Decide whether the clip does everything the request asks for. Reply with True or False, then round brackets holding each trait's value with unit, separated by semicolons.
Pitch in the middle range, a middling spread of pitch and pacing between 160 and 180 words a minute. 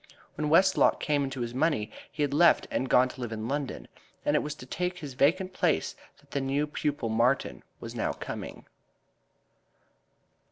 True (145 Hz; 3.2 semitones; 175 wpm)